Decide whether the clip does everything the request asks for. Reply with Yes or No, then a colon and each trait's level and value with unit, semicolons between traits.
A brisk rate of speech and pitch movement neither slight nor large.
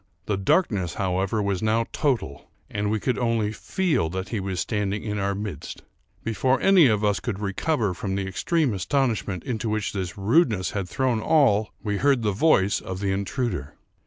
No: average, 185 wpm; average, 3.8 semitones